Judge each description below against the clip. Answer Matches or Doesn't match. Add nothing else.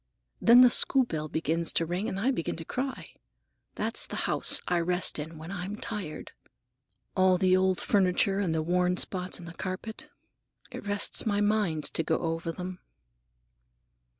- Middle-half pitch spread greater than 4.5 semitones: Doesn't match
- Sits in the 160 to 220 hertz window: Matches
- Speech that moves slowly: Doesn't match